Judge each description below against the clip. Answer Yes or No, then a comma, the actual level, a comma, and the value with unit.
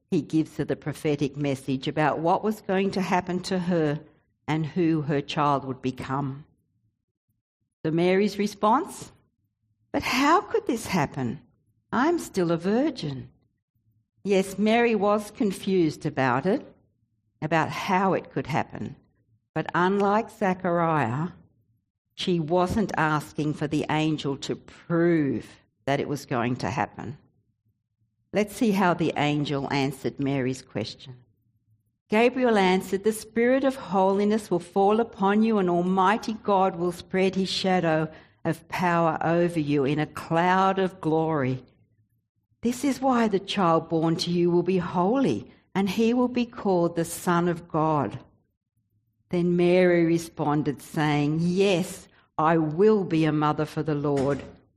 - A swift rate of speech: No, average, 140 wpm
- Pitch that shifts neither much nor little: No, wide, 6.0 semitones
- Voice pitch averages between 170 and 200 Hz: No, medium, 160 Hz